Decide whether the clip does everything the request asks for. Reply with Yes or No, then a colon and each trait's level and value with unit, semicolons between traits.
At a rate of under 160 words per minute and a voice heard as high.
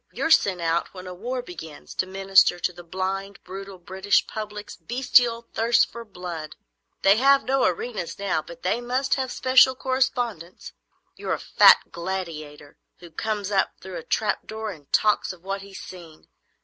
No: average, 170 wpm; high, 195 Hz